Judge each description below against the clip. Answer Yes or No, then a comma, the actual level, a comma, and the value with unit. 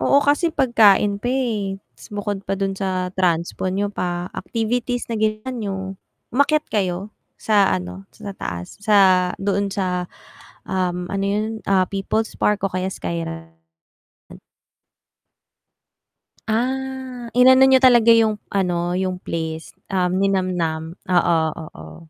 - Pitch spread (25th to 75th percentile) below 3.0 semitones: No, average, 4.0 semitones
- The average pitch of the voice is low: No, high, 195 Hz